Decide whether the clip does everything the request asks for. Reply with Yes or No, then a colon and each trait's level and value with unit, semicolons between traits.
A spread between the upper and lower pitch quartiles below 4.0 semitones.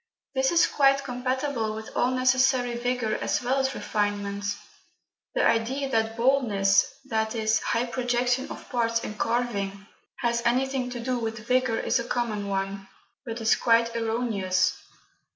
Yes: narrow, 2.6 semitones